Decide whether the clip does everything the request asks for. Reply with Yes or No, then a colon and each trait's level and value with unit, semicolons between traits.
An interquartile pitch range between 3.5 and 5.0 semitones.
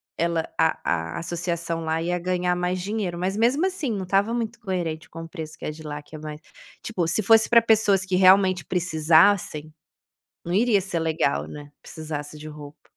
Yes: average, 3.8 semitones